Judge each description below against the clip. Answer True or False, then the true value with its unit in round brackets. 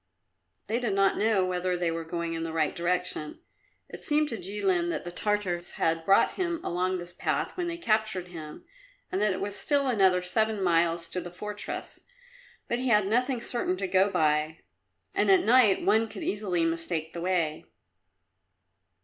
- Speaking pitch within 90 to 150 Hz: False (185 Hz)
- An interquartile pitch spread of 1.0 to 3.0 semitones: False (3.8 semitones)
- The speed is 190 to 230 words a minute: False (180 wpm)